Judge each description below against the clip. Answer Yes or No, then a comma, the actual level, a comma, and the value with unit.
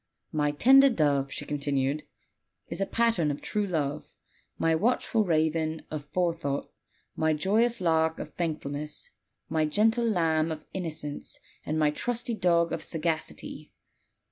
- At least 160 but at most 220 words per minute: No, slow, 135 wpm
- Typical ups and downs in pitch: Yes, average, 4.2 semitones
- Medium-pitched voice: Yes, medium, 160 Hz